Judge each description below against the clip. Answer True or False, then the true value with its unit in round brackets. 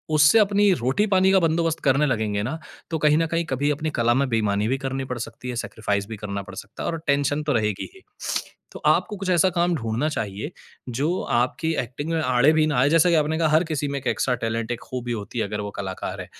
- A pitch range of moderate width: False (6.0 semitones)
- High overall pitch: False (140 Hz)